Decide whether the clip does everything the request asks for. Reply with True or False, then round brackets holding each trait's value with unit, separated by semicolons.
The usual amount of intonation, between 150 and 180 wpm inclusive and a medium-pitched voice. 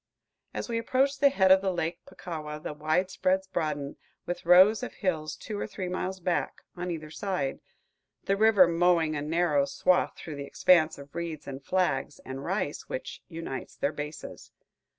True (3.8 semitones; 170 wpm; 170 Hz)